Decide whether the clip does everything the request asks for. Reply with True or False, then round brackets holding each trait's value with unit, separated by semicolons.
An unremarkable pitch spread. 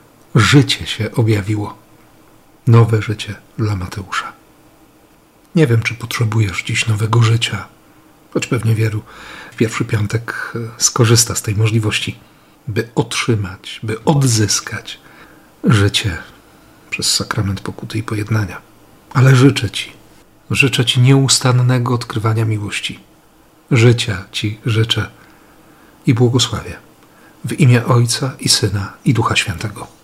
True (3.3 semitones)